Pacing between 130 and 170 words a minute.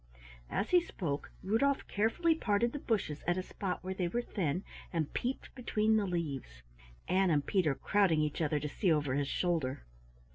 No: average, 180 wpm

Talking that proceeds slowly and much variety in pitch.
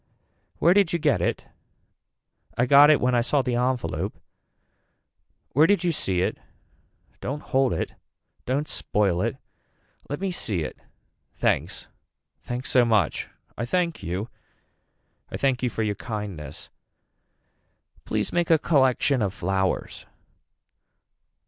Yes: slow, 130 wpm; wide, 6.0 semitones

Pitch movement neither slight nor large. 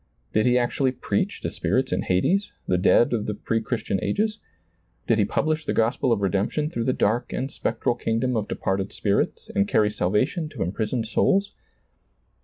Yes: average, 4.2 semitones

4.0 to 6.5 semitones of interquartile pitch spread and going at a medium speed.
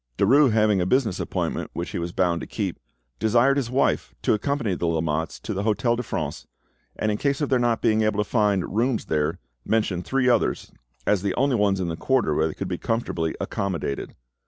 No: wide, 5.4 semitones; fast, 210 wpm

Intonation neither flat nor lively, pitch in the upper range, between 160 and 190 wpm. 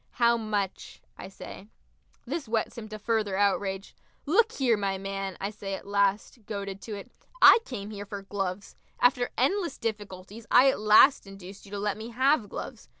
Yes: average, 3.1 semitones; high, 210 Hz; average, 180 wpm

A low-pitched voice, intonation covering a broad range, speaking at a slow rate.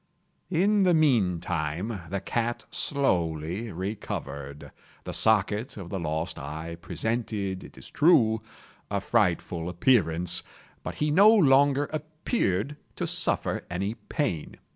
Yes: low, 105 Hz; wide, 8.4 semitones; slow, 120 wpm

